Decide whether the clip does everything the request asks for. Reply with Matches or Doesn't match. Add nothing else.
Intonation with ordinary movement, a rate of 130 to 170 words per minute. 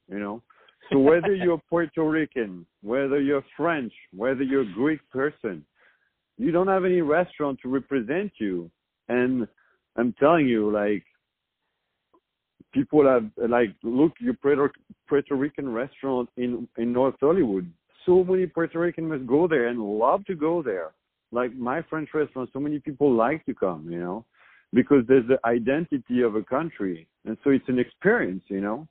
Matches